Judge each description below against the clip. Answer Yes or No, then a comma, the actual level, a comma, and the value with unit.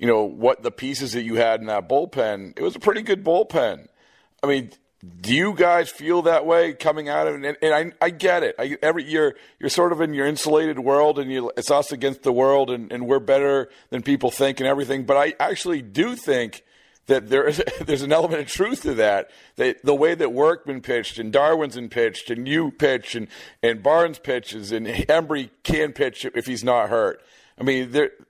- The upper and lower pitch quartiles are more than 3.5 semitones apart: Yes, average, 4.7 semitones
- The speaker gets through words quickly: Yes, fast, 215 wpm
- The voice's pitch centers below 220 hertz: Yes, medium, 140 Hz